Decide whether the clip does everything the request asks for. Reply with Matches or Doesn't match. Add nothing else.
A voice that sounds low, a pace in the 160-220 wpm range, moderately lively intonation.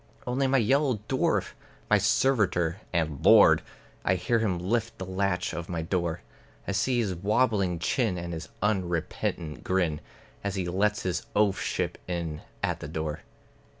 Doesn't match